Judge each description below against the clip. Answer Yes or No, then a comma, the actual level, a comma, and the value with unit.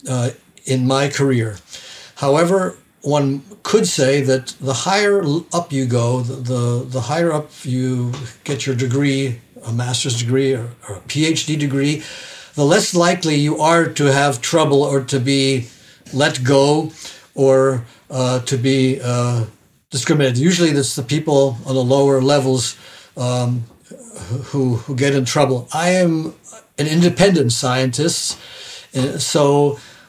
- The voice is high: No, low, 135 Hz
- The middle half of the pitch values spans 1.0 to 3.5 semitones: Yes, average, 3.1 semitones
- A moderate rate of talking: Yes, average, 140 wpm